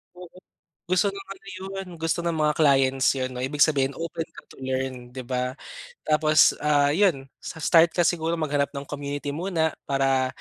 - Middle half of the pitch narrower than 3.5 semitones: No, average, 3.8 semitones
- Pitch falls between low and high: Yes, medium, 150 Hz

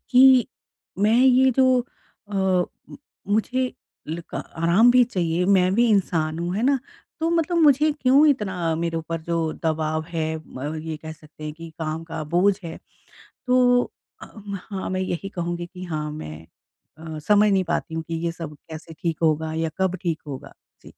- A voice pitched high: No, medium, 175 Hz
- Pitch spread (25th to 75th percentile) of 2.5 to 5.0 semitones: No, wide, 5.5 semitones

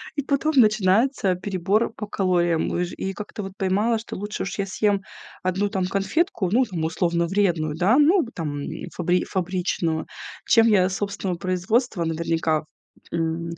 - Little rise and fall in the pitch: No, average, 3.6 semitones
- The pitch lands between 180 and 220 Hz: Yes, high, 190 Hz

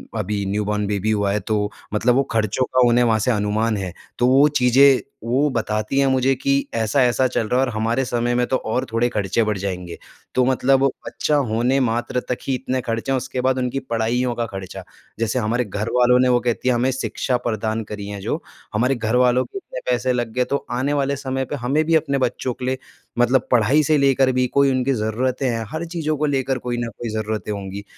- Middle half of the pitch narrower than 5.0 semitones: Yes, average, 3.2 semitones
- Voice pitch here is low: Yes, low, 125 Hz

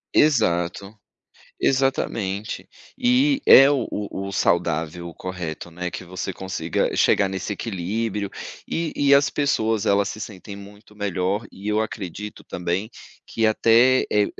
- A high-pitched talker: No, low, 100 Hz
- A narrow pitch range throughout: No, average, 3.8 semitones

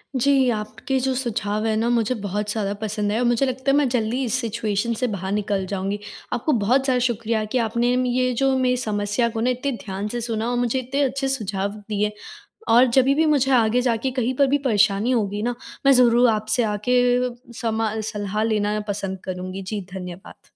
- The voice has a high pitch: Yes, high, 230 Hz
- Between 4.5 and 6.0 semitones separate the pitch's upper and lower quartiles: No, average, 3.4 semitones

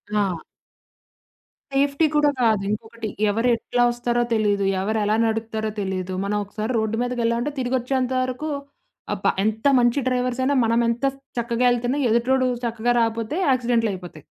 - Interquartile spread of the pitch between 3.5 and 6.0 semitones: No, narrow, 2.4 semitones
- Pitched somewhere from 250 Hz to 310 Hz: No, high, 235 Hz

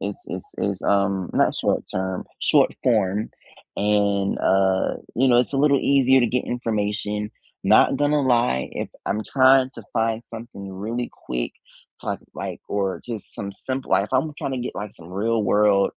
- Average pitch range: Yes, average, 3.9 semitones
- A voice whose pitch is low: Yes, low, 105 Hz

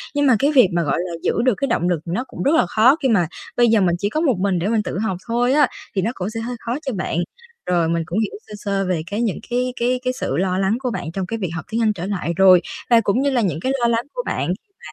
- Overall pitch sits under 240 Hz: Yes, high, 220 Hz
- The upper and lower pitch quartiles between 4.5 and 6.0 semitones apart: Yes, average, 5.3 semitones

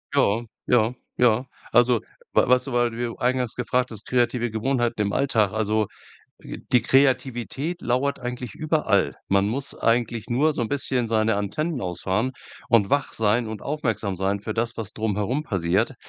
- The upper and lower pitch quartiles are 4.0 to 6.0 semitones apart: No, average, 2.9 semitones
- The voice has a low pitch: Yes, low, 120 Hz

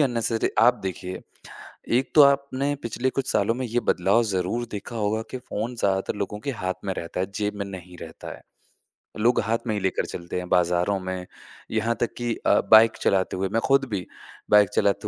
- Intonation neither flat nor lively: Yes, average, 4.1 semitones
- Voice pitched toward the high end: No, low, 105 Hz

